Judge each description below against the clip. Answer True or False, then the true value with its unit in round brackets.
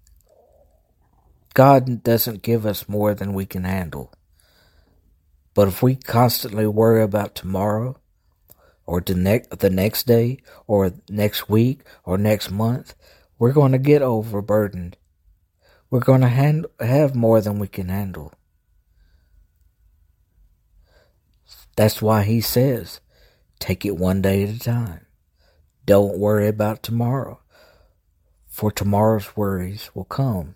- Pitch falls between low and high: False (100 Hz)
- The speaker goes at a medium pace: False (125 wpm)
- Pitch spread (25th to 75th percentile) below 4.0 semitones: False (4.5 semitones)